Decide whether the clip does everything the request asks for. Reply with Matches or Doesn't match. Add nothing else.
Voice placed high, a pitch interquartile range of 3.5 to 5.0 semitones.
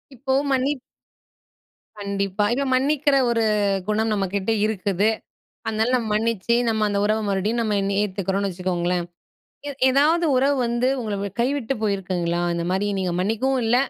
Matches